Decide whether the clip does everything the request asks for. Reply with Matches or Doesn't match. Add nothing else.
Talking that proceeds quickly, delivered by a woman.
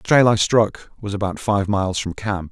Doesn't match